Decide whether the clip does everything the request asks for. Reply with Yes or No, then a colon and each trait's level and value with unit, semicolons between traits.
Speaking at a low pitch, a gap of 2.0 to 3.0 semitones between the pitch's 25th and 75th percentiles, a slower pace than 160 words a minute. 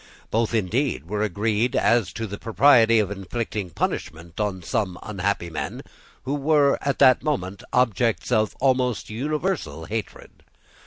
No: low, 110 Hz; average, 4.3 semitones; average, 140 wpm